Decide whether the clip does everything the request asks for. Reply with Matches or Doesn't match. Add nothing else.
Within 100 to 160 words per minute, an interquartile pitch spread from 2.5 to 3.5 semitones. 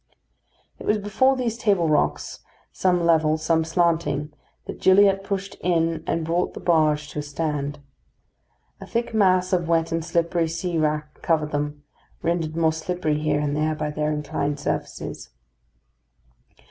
Matches